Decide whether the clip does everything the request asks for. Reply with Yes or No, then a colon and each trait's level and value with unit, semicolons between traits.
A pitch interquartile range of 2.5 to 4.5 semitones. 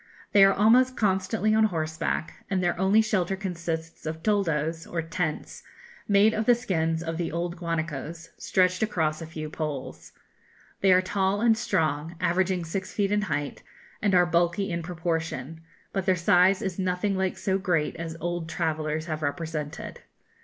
Yes: average, 3.1 semitones